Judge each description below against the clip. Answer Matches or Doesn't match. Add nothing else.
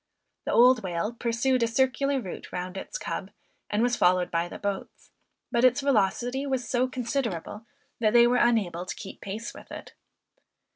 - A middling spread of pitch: Matches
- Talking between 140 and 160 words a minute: Doesn't match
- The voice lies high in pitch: Matches